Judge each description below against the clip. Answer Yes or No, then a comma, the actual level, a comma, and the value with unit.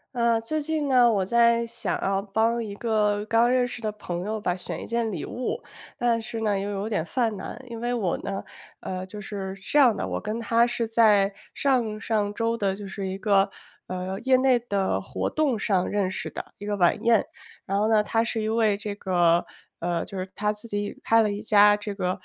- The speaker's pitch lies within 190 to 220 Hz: Yes, high, 210 Hz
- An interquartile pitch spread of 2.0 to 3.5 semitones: Yes, average, 2.8 semitones